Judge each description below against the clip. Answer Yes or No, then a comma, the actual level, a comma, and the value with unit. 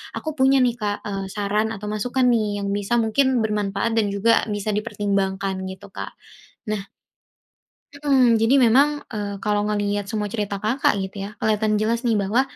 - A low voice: No, high, 210 Hz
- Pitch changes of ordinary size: No, narrow, 2.3 semitones